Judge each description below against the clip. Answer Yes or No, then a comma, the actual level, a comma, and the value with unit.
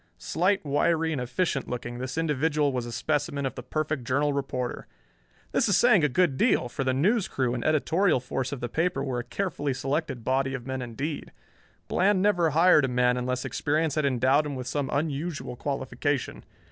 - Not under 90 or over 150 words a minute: No, average, 190 wpm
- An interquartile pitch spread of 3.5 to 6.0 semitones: Yes, average, 3.8 semitones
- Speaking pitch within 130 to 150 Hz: Yes, medium, 140 Hz